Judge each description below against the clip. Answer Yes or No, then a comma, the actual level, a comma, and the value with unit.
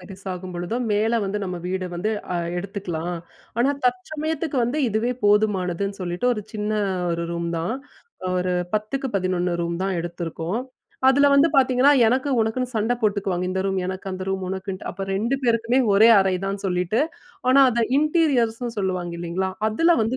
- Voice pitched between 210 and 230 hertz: No, high, 200 Hz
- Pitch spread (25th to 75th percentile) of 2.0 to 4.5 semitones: No, average, 4.9 semitones